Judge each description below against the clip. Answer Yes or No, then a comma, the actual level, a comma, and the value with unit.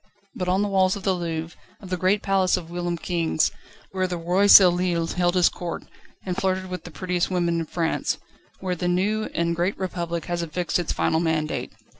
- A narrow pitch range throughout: Yes, narrow, 1.7 semitones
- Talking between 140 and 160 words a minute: No, average, 200 wpm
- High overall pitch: No, medium, 180 Hz